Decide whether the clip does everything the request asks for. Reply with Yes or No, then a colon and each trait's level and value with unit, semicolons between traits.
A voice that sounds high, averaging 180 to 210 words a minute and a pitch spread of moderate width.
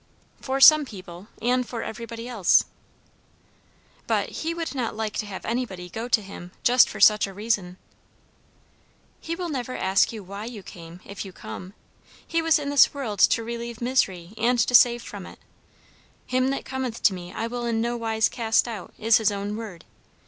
Yes: high, 230 Hz; average, 185 wpm; average, 3.7 semitones